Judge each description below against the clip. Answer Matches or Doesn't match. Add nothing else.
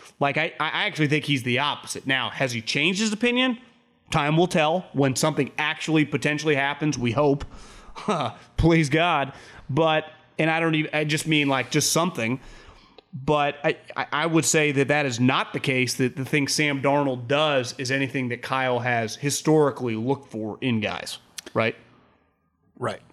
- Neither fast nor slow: Matches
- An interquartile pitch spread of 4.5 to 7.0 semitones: Doesn't match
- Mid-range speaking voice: Matches